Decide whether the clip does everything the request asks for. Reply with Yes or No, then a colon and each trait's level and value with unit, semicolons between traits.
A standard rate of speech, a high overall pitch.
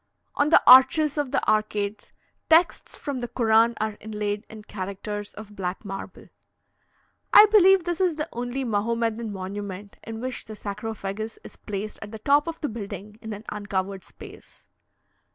Yes: average, 160 wpm; high, 220 Hz